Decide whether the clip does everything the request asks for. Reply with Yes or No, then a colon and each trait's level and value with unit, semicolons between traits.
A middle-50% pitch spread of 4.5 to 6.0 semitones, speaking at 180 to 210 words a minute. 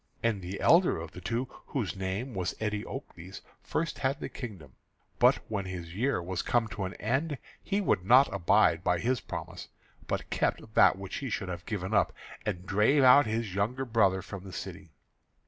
Yes: average, 5.2 semitones; average, 185 wpm